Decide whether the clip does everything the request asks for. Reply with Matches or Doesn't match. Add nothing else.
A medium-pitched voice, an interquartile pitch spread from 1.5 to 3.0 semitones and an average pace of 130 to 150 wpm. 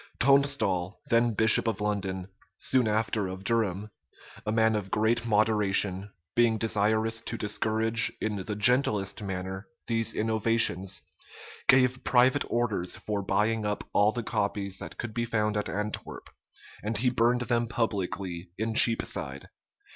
Doesn't match